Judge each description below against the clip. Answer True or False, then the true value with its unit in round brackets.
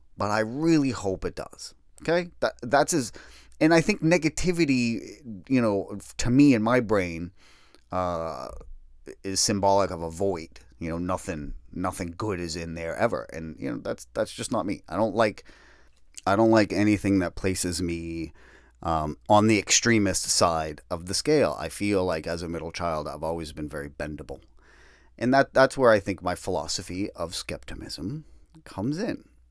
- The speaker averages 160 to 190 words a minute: True (175 wpm)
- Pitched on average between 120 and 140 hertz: False (95 Hz)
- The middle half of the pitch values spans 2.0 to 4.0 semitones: False (5.0 semitones)